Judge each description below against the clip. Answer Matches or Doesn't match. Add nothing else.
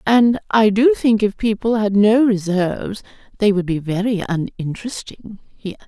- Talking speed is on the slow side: Doesn't match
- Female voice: Matches